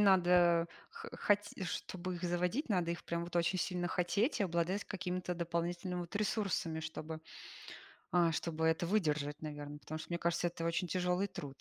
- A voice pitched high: No, medium, 175 Hz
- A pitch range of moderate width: No, narrow, 1.8 semitones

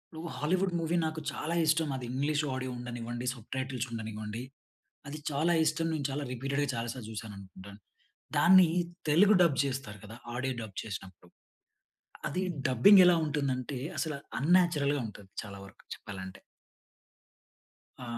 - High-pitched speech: No, low, 135 Hz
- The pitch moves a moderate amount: No, wide, 5.7 semitones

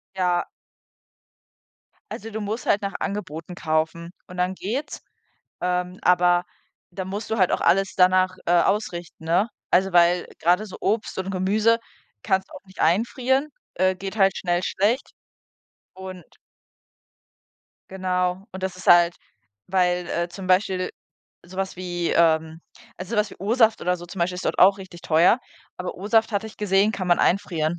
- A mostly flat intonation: Yes, narrow, 2.2 semitones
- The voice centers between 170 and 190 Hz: Yes, medium, 185 Hz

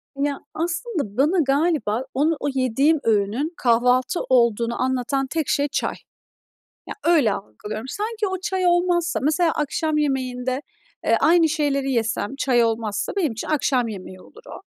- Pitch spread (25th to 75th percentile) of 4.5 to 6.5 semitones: Yes, wide, 5.5 semitones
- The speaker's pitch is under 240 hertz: No, very high, 275 Hz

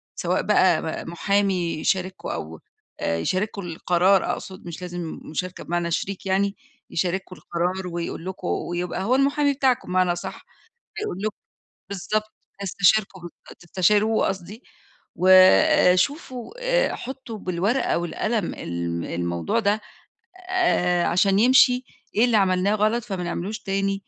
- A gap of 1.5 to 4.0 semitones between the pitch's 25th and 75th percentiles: Yes, average, 3.6 semitones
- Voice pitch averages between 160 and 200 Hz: Yes, high, 190 Hz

